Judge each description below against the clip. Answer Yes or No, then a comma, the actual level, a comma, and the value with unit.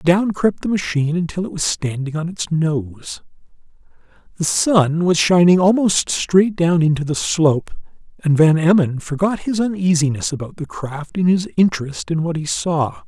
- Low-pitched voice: No, medium, 165 Hz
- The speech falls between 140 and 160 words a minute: No, average, 170 wpm